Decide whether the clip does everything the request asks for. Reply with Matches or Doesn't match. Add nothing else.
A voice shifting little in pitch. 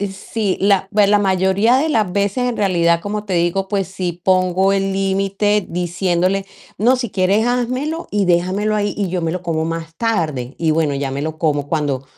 Doesn't match